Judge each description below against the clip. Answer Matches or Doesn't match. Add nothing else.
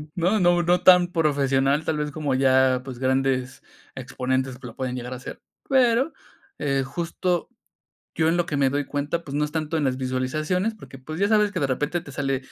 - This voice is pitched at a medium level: Matches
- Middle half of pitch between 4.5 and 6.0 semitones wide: Matches